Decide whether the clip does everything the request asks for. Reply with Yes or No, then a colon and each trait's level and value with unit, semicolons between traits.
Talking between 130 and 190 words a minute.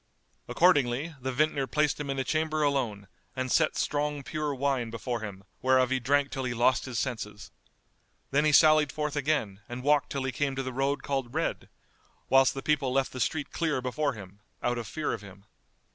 No: average, 200 wpm